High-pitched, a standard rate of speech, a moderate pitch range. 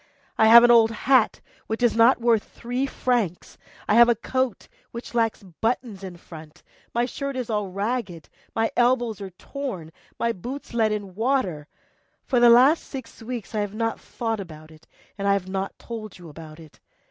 Yes: high, 225 Hz; average, 190 wpm; average, 3.9 semitones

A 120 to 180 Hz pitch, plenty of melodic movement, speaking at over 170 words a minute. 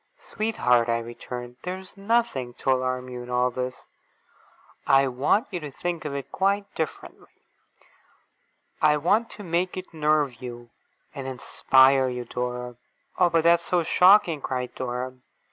No: low, 135 Hz; wide, 5.8 semitones; average, 150 wpm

